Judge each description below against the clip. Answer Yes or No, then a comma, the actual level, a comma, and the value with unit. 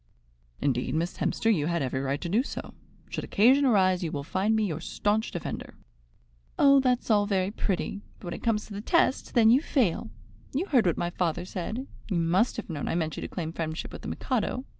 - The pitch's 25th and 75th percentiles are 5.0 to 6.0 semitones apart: Yes, average, 5.3 semitones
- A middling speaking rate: No, fast, 220 wpm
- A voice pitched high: Yes, high, 195 Hz